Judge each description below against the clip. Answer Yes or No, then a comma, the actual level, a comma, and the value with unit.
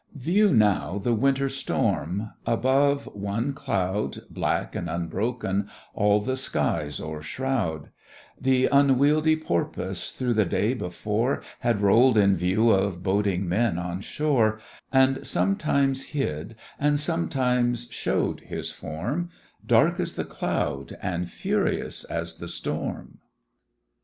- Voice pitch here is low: Yes, low, 110 Hz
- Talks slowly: Yes, slow, 120 wpm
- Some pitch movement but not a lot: No, wide, 6.1 semitones